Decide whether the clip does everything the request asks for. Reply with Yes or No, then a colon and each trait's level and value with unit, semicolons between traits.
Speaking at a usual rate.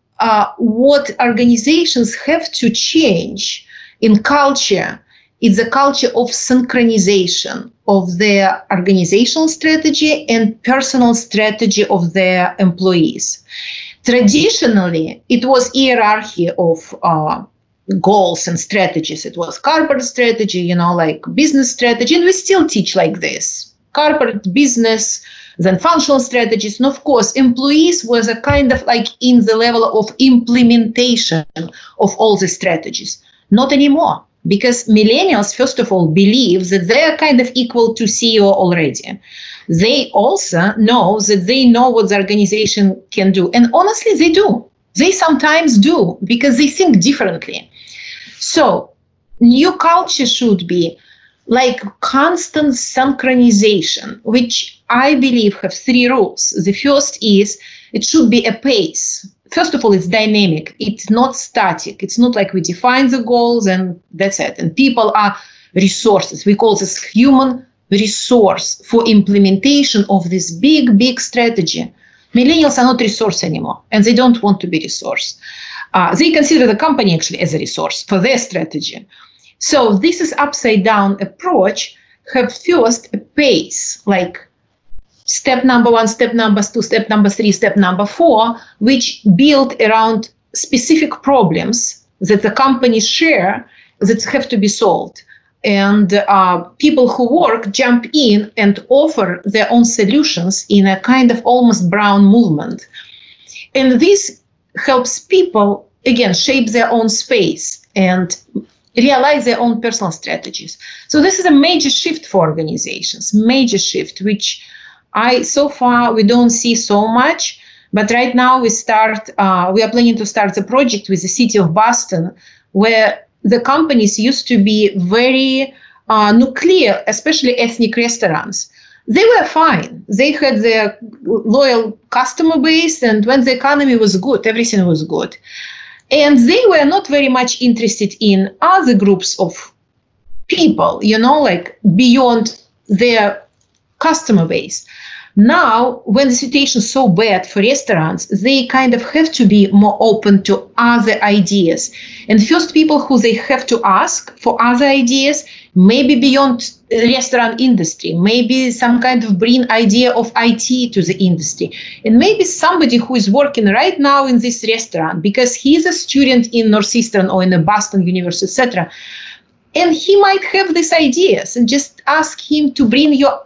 Yes: average, 150 wpm